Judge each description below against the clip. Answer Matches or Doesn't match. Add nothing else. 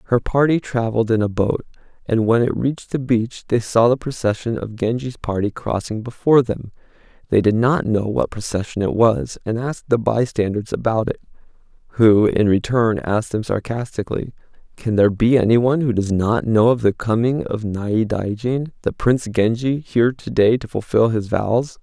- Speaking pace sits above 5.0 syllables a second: Matches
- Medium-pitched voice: Doesn't match